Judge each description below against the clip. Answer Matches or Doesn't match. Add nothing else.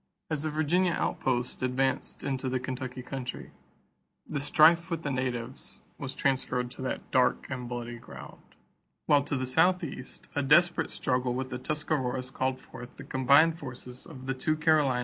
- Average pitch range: Matches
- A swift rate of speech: Doesn't match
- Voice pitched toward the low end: Matches